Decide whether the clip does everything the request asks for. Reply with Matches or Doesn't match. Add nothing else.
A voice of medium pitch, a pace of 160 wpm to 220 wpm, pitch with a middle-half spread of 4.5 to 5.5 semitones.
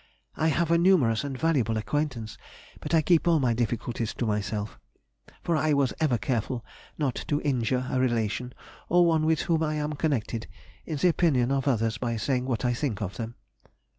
Doesn't match